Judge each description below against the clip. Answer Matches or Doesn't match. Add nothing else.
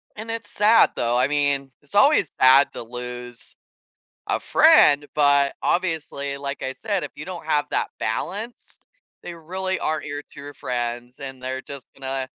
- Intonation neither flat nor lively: Matches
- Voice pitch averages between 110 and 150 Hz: Matches